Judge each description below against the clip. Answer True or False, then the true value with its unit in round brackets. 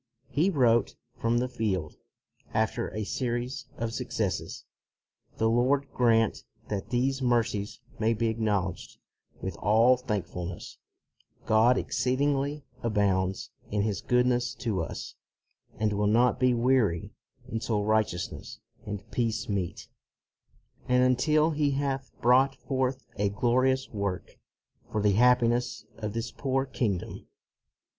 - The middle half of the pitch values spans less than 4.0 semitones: True (3.4 semitones)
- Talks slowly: True (125 wpm)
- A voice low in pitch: True (115 Hz)